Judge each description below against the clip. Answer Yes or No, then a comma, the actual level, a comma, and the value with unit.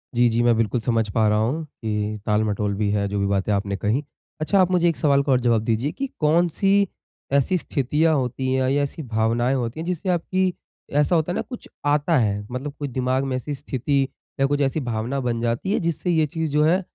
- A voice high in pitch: No, low, 135 Hz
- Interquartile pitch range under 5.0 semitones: No, wide, 5.5 semitones